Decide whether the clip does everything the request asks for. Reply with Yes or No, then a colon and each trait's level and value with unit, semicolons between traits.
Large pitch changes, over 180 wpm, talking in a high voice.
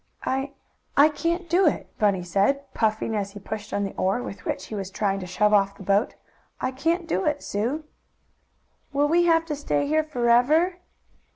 Yes: wide, 7.3 semitones; average, 190 wpm; high, 245 Hz